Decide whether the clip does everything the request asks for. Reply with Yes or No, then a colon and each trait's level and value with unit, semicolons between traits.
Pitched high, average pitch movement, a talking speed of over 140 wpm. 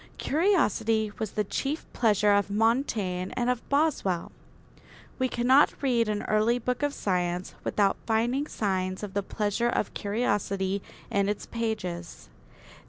No: high, 215 Hz; average, 3.7 semitones; slow, 135 wpm